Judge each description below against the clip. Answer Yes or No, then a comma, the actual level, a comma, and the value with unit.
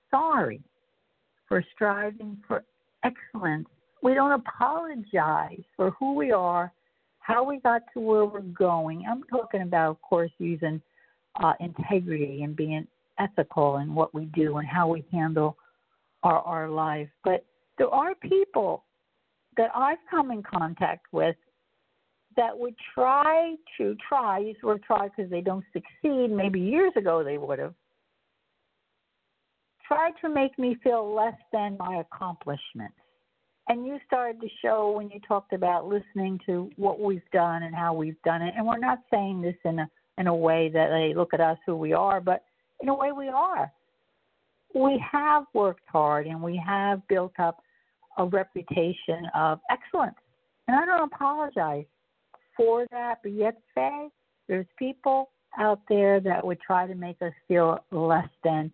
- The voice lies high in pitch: Yes, high, 200 Hz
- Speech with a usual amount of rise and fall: No, wide, 6.7 semitones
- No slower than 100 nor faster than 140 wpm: No, average, 160 wpm